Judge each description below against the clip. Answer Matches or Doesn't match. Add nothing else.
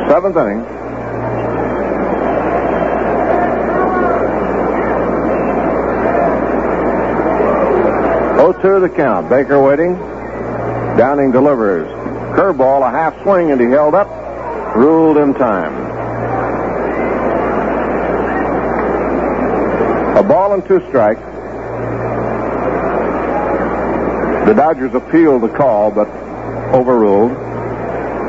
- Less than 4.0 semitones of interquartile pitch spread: Doesn't match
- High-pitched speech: Doesn't match